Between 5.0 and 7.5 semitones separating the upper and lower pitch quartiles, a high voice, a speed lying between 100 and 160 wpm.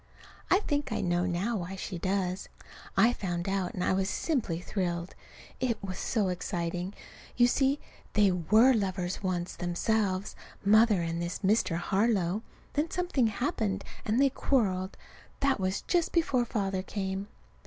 No: average, 4.3 semitones; high, 195 Hz; average, 150 wpm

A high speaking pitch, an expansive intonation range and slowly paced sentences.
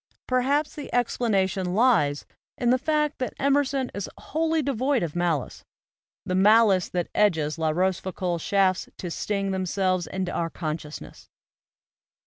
Yes: high, 195 Hz; wide, 6.4 semitones; slow, 130 wpm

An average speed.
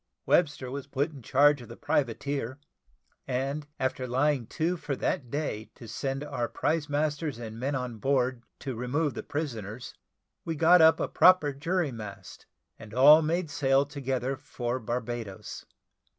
Yes: average, 155 wpm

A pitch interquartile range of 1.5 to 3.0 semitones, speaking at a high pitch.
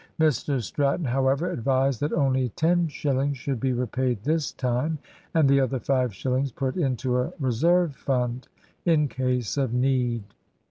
No: narrow, 2.4 semitones; low, 135 Hz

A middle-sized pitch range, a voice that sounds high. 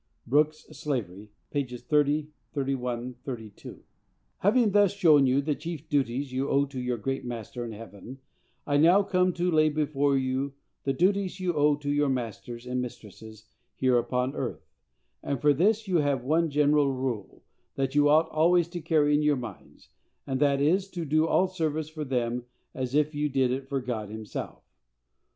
No: average, 3.7 semitones; medium, 140 Hz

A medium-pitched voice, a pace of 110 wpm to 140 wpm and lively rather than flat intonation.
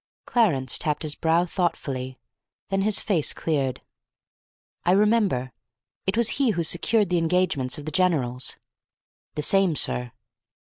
Yes: medium, 170 Hz; slow, 135 wpm; wide, 5.9 semitones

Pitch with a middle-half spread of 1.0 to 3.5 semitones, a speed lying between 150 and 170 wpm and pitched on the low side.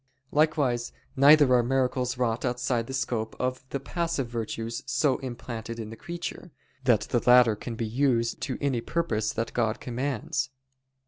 Yes: narrow, 2.6 semitones; average, 155 wpm; low, 125 Hz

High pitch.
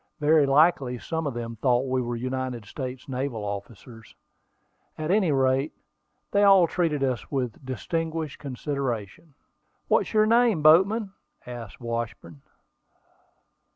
No: low, 135 Hz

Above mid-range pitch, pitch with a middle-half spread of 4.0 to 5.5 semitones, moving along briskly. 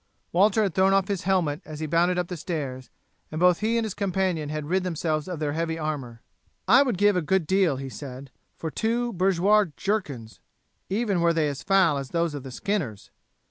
No: medium, 170 Hz; average, 4.4 semitones; fast, 210 wpm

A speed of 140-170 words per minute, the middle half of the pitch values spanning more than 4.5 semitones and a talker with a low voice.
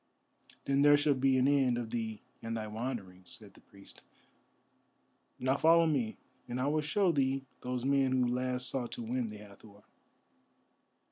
No: average, 165 wpm; average, 3.3 semitones; low, 125 Hz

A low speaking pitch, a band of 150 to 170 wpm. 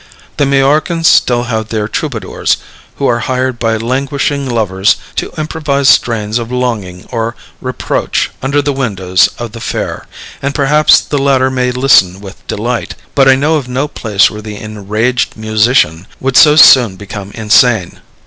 Yes: low, 125 Hz; average, 160 wpm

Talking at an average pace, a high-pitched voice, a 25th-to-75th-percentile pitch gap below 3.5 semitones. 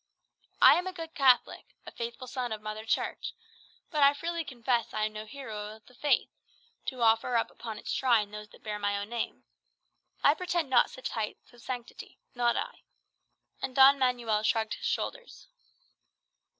No: average, 180 wpm; high, 240 Hz; average, 4.0 semitones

